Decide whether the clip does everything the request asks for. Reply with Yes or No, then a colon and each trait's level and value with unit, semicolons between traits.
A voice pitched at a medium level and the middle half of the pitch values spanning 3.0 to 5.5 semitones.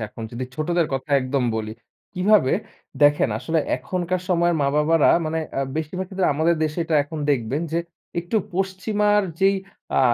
Yes: medium, 160 Hz; average, 4.5 semitones